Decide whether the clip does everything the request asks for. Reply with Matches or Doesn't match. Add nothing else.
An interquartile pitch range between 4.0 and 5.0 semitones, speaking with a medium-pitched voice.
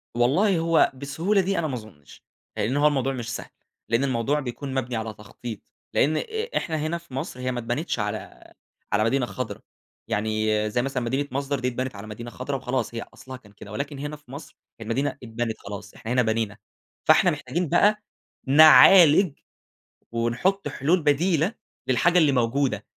Doesn't match